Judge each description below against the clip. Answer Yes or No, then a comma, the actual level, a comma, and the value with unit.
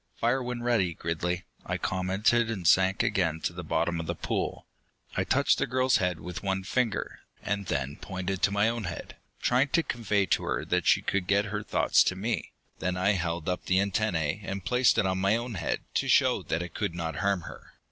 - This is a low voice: Yes, very low, 95 Hz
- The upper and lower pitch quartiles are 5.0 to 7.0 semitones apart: No, average, 3.6 semitones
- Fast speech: Yes, fast, 215 wpm